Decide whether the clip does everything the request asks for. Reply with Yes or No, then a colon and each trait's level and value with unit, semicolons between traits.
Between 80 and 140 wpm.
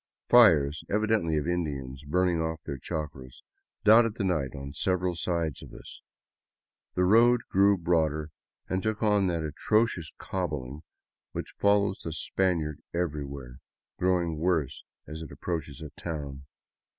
Yes: slow, 135 wpm